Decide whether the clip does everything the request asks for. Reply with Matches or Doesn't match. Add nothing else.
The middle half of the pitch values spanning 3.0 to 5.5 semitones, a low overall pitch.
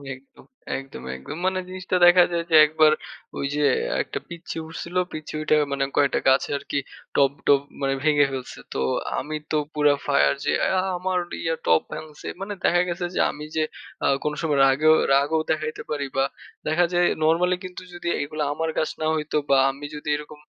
Doesn't match